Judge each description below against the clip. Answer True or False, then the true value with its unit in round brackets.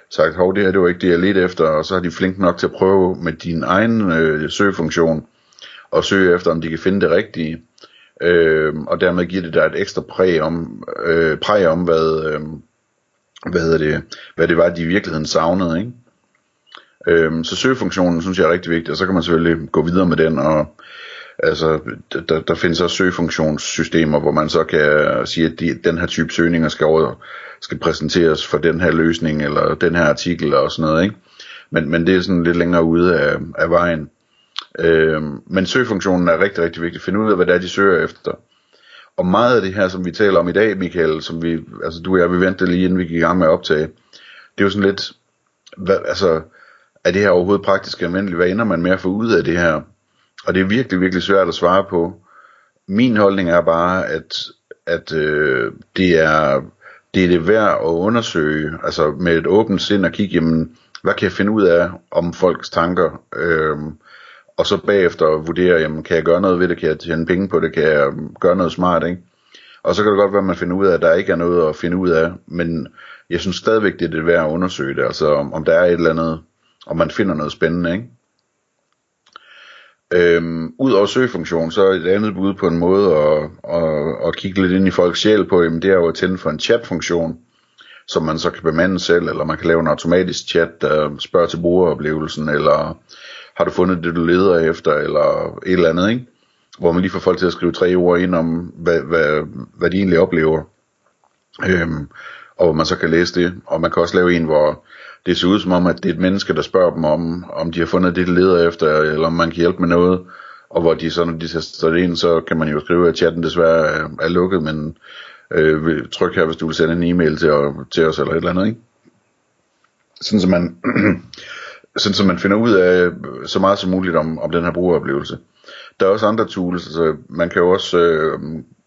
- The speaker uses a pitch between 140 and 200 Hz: False (85 Hz)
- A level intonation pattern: True (2.3 semitones)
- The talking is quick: True (230 wpm)